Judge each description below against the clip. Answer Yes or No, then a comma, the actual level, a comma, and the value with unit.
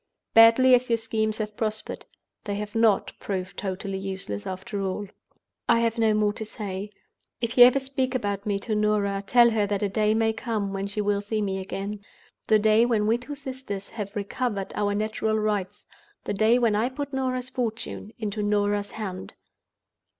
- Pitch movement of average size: No, narrow, 2.2 semitones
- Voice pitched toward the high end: Yes, high, 215 Hz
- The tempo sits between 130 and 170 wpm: No, average, 180 wpm